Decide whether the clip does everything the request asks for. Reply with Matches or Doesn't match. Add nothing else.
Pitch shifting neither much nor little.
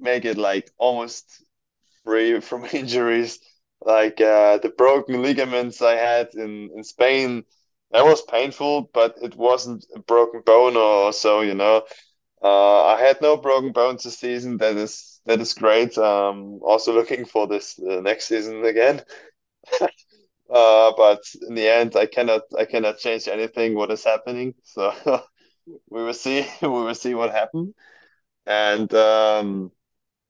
Doesn't match